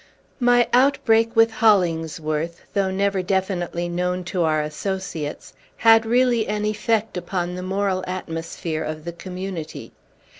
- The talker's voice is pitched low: No, medium, 185 Hz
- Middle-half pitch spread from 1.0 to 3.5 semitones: No, average, 3.9 semitones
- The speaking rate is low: Yes, slow, 125 wpm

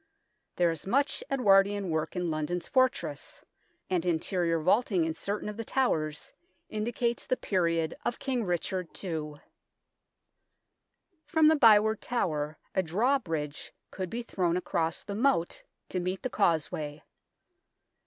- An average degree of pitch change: No, wide, 5.7 semitones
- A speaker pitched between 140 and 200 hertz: Yes, medium, 185 Hz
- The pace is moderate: No, slow, 130 wpm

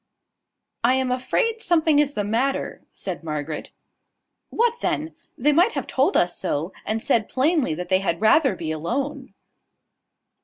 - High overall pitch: Yes, very high, 255 Hz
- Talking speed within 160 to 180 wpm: No, average, 150 wpm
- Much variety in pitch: Yes, wide, 8.4 semitones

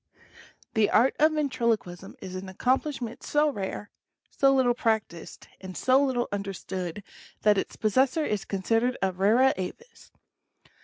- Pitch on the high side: Yes, high, 225 Hz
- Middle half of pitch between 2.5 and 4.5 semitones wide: No, wide, 5.4 semitones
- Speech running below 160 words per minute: Yes, average, 140 wpm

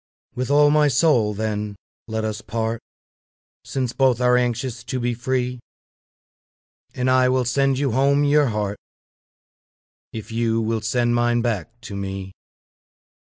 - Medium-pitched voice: No, low, 120 Hz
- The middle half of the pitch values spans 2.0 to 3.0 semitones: Yes, average, 2.7 semitones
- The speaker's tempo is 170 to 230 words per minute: No, average, 140 wpm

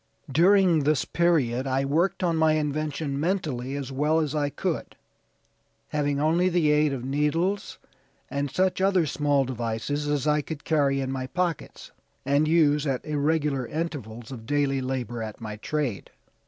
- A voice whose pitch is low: No, medium, 145 Hz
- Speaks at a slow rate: No, average, 155 wpm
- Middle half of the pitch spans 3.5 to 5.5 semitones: No, average, 3.0 semitones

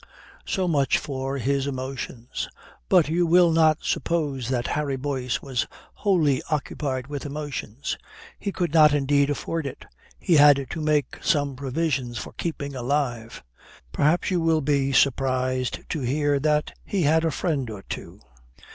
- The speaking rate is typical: Yes, average, 150 wpm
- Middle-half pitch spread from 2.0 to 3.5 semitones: Yes, average, 2.9 semitones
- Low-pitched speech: No, medium, 145 Hz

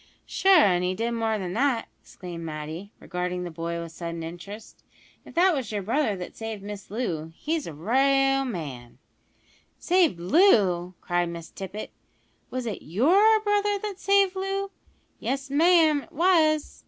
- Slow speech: No, average, 160 wpm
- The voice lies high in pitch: Yes, high, 225 Hz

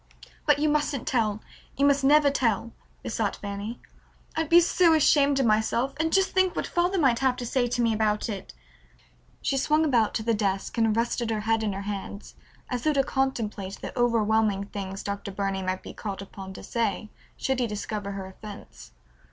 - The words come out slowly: No, average, 195 wpm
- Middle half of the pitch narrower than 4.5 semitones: No, average, 5.2 semitones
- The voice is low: No, high, 230 Hz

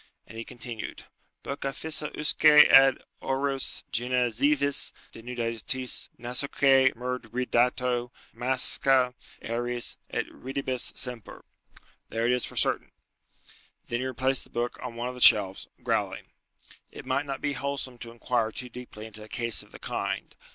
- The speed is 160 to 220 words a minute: No, average, 140 wpm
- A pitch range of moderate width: No, narrow, 2.1 semitones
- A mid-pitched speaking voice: No, low, 125 Hz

